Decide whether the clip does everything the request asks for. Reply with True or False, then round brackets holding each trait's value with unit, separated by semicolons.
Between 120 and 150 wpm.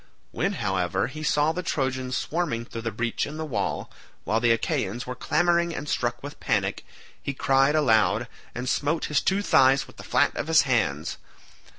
False (185 wpm)